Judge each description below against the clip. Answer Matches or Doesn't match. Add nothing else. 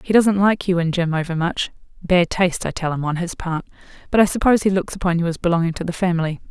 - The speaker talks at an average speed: Doesn't match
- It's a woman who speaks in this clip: Matches